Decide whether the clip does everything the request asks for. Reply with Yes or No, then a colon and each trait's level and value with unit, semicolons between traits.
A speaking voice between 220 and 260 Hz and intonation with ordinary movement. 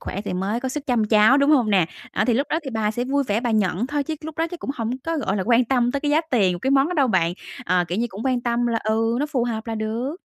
Yes: high, 240 Hz; average, 4.0 semitones